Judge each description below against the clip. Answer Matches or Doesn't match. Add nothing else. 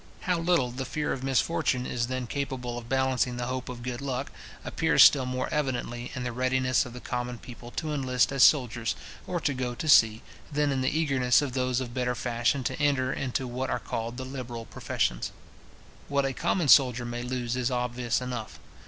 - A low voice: Matches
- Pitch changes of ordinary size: Doesn't match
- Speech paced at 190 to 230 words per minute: Matches